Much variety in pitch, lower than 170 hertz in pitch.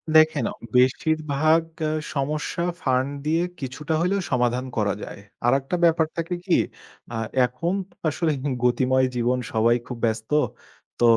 No: average, 4.3 semitones; low, 135 Hz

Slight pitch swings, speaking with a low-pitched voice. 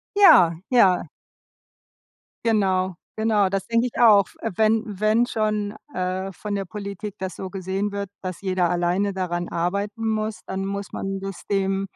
No: narrow, 2.3 semitones; high, 195 Hz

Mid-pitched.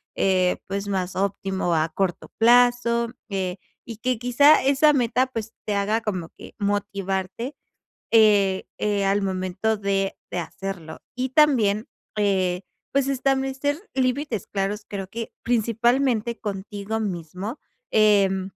No: high, 205 Hz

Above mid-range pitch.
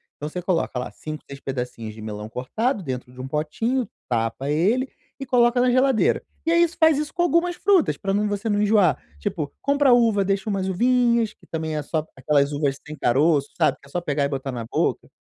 No: medium, 180 Hz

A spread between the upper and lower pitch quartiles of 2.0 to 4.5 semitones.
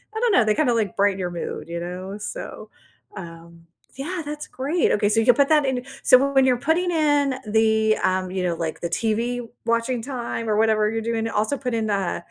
No: average, 5.0 semitones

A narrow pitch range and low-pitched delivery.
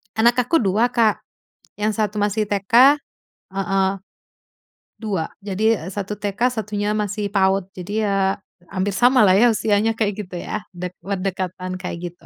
No: narrow, 2.3 semitones; high, 205 Hz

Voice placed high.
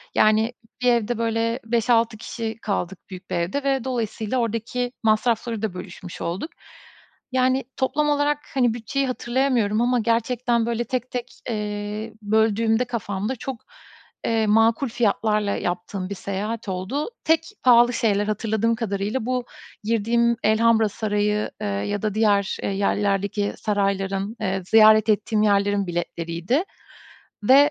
Yes: high, 220 Hz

